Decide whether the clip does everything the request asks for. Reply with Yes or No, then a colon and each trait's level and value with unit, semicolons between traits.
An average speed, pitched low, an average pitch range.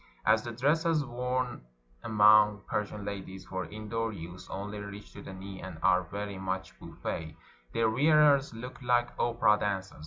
Yes: average, 155 wpm; low, 105 Hz; average, 3.9 semitones